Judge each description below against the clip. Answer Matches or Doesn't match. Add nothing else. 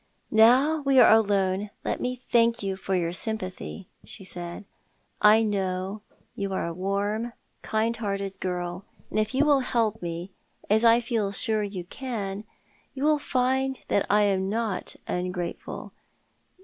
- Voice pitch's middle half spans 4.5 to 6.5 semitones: Doesn't match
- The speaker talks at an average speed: Matches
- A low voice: Doesn't match